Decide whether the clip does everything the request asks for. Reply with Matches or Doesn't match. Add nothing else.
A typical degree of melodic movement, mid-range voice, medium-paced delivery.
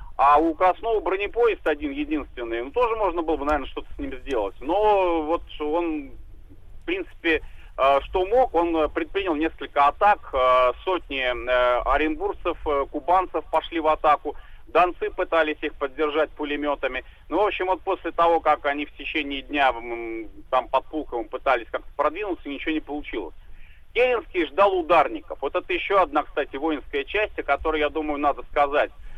Matches